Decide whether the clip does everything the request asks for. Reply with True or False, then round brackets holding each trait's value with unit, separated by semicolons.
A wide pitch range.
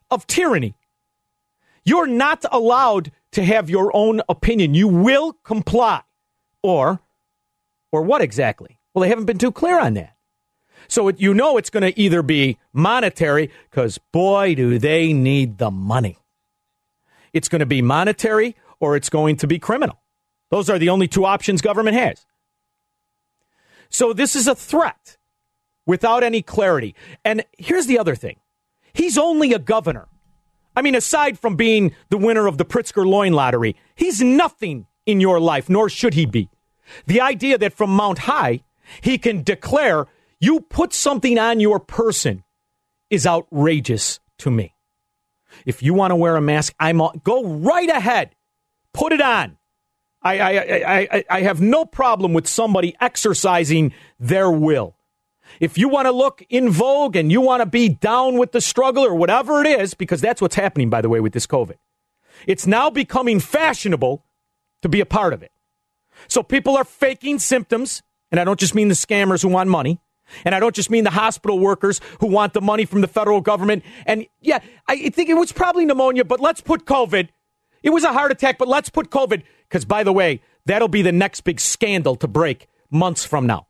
True (8.3 semitones)